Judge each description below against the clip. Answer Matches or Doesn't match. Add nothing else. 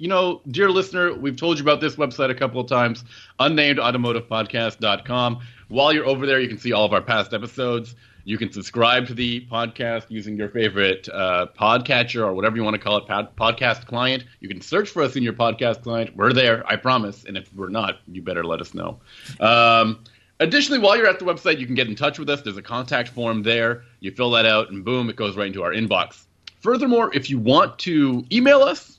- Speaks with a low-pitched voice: Matches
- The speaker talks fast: Matches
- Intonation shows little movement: Doesn't match